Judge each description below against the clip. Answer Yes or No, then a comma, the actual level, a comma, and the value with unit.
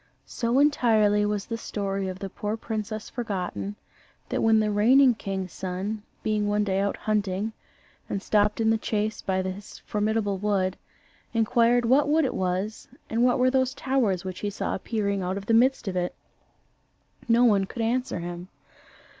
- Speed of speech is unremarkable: Yes, average, 170 wpm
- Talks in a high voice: Yes, high, 210 Hz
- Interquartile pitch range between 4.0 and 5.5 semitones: No, average, 2.9 semitones